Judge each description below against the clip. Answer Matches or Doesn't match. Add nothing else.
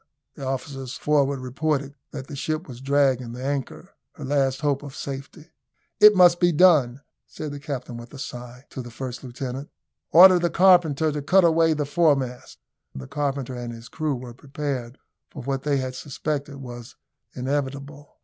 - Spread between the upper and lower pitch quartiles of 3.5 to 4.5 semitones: Doesn't match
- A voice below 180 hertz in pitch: Matches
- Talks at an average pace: Matches